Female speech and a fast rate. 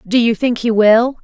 Yes: female; fast, 245 wpm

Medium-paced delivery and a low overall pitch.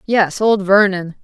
No: average, 145 wpm; high, 195 Hz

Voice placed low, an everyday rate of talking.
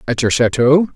Yes: low, 130 Hz; average, 190 wpm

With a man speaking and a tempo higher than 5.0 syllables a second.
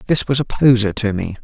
Yes: male; 5.7 syllables/s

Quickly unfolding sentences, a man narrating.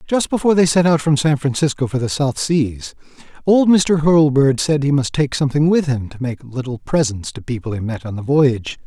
Yes: fast, 225 wpm; male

